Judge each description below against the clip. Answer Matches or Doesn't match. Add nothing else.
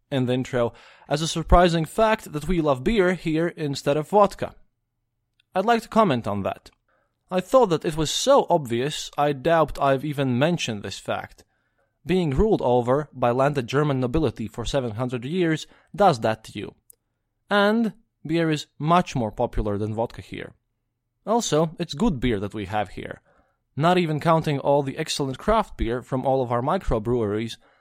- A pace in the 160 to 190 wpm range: Matches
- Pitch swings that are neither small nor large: Doesn't match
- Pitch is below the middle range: Doesn't match